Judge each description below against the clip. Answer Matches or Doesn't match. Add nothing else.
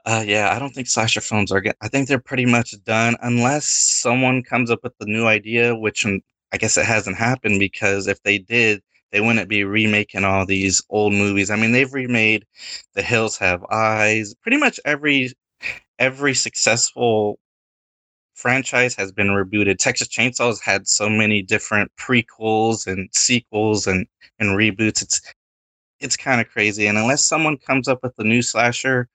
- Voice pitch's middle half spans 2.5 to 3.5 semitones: Matches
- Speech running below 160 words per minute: Doesn't match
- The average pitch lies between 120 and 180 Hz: Doesn't match